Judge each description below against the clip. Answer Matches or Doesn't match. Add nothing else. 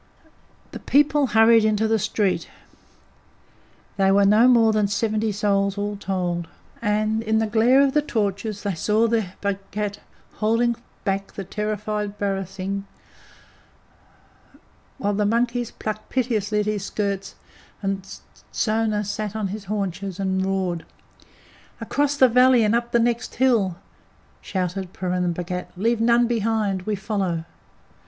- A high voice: Matches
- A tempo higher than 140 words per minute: Doesn't match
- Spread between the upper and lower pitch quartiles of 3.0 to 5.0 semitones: Doesn't match